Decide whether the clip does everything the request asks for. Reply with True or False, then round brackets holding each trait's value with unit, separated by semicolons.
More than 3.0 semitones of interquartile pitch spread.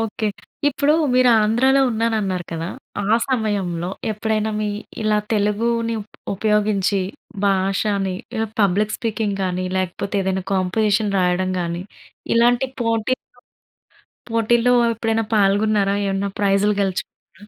False (2.6 semitones)